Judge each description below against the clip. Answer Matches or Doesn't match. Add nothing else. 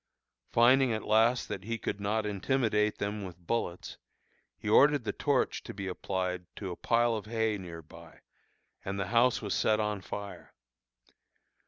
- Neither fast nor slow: Matches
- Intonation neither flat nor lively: Matches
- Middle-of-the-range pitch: Doesn't match